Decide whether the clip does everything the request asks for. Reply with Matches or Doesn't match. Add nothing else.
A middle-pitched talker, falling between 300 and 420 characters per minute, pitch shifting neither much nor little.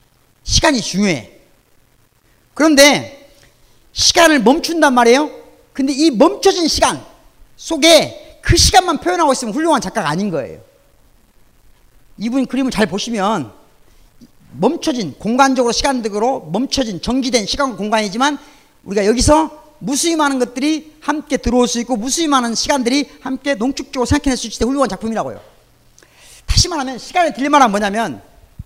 Doesn't match